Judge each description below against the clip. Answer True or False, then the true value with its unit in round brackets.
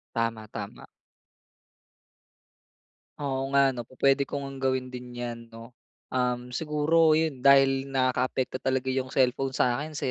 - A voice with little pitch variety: True (1.8 semitones)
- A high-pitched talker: False (130 Hz)